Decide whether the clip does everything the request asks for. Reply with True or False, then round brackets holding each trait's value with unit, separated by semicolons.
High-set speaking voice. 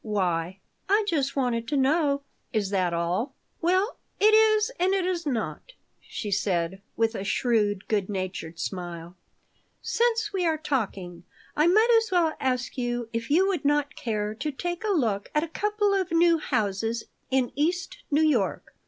True (265 Hz)